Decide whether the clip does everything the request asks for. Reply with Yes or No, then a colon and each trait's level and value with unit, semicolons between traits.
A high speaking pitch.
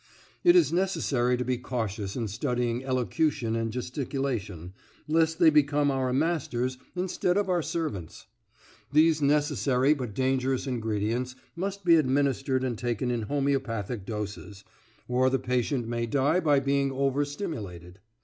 No: low, 130 Hz